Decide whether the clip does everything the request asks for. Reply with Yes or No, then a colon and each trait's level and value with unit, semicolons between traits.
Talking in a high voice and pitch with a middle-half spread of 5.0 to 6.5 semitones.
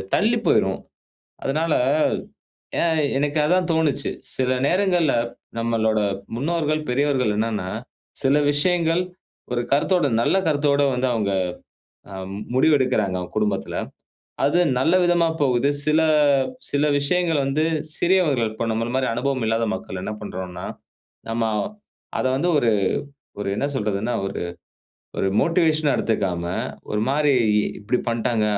No: low, 135 Hz; wide, 5.6 semitones